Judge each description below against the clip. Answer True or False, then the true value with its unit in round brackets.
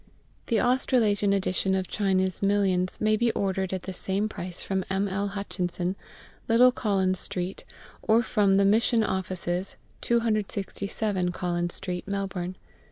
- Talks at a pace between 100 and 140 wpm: True (135 wpm)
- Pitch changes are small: True (2.1 semitones)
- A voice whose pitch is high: True (195 Hz)